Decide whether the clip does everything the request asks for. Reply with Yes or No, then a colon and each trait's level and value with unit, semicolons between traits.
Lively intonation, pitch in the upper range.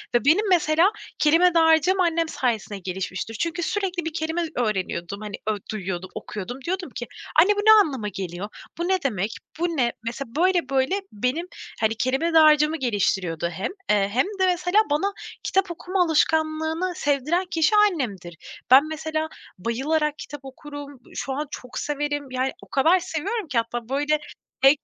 Yes: wide, 6.4 semitones; very high, 295 Hz